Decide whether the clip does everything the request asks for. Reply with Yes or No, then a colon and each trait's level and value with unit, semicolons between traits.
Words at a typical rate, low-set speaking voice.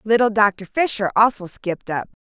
No: average, 160 wpm; high, 210 Hz